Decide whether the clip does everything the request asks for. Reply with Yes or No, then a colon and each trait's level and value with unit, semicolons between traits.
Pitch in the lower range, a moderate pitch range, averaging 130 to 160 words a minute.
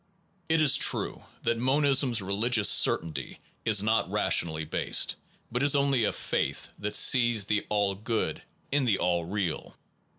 Yes: low, 110 Hz; average, 4.8 semitones; average, 155 wpm